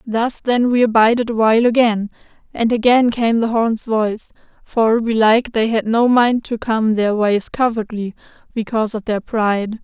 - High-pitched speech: Yes, high, 225 Hz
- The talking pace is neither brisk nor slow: Yes, average, 170 wpm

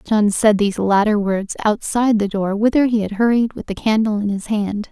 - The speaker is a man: No, female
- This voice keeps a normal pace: No, fast, 220 wpm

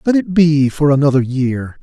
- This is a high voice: No, medium, 150 Hz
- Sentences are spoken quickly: No, average, 195 wpm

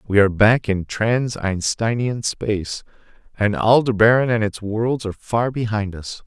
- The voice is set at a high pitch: No, low, 110 Hz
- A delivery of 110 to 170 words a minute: Yes, average, 155 wpm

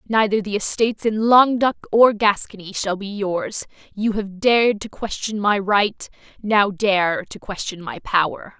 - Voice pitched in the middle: No, high, 205 Hz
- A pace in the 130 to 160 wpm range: Yes, average, 155 wpm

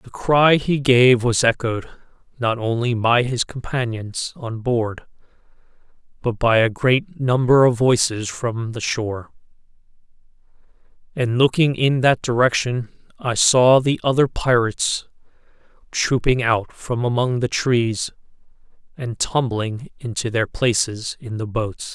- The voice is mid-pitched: No, low, 120 Hz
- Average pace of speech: No, slow, 130 wpm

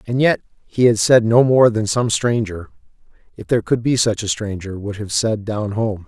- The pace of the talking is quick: Yes, fast, 215 wpm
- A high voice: No, low, 110 Hz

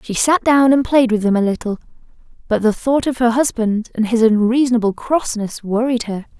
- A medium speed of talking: Yes, average, 195 wpm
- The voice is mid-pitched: No, high, 235 Hz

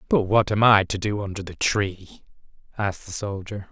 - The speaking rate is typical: Yes, average, 195 wpm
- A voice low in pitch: Yes, low, 100 Hz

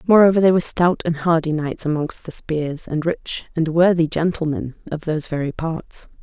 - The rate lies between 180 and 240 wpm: Yes, average, 185 wpm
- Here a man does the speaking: No, female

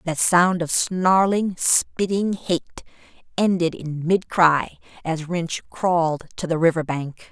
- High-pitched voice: No, medium, 170 Hz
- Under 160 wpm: Yes, average, 140 wpm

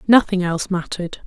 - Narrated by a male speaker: No, female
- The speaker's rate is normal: Yes, average, 145 wpm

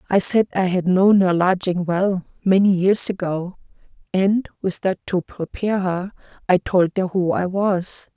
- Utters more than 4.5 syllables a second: No, 4.3 syllables/s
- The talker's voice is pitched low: No, medium, 185 Hz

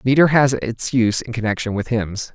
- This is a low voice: Yes, low, 115 Hz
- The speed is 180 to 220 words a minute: Yes, fast, 205 wpm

